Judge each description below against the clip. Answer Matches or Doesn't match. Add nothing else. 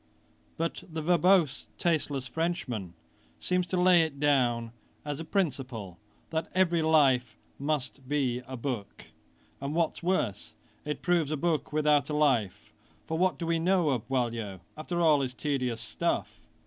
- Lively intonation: Doesn't match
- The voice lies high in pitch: Doesn't match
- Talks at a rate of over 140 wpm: Matches